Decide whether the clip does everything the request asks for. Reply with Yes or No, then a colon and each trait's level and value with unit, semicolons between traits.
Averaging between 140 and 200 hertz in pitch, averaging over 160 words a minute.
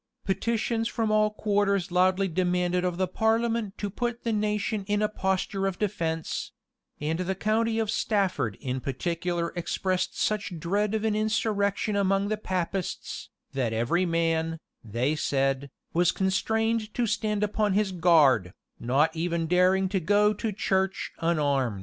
No: high, 190 Hz; average, 150 wpm